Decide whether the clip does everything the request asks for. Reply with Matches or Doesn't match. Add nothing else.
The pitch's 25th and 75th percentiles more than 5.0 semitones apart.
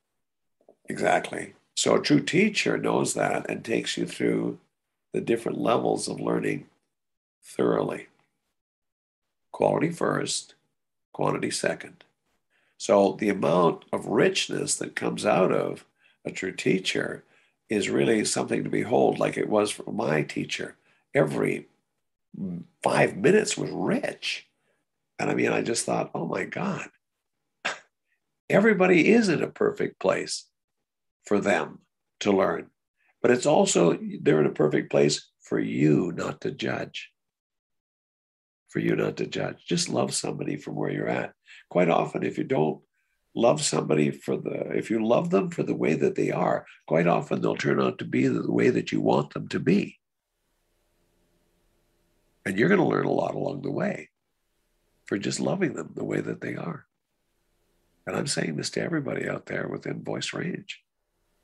Doesn't match